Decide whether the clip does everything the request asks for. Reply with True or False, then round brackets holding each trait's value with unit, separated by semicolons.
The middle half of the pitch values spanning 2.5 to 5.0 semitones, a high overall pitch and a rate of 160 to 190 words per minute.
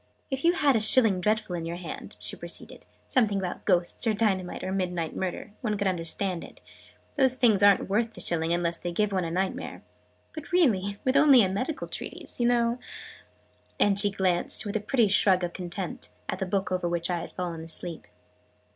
False (4.0 semitones; 195 Hz; 205 wpm)